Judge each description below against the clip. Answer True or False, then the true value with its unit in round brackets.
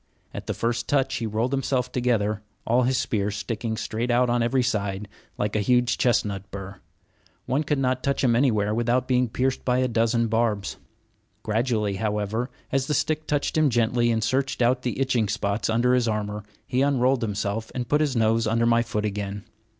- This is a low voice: True (115 Hz)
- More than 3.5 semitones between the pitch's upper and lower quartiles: False (3.1 semitones)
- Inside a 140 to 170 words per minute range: False (190 wpm)